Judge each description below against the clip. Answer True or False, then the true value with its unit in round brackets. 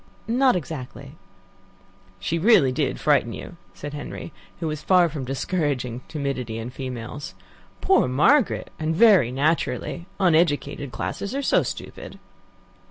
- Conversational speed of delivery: False (125 wpm)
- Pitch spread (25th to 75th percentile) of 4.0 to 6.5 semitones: True (5.1 semitones)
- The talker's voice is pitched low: False (150 Hz)